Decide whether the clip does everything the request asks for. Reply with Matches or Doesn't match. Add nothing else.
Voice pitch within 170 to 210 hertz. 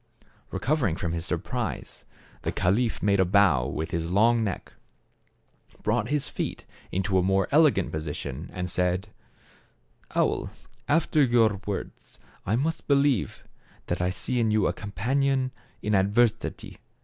Doesn't match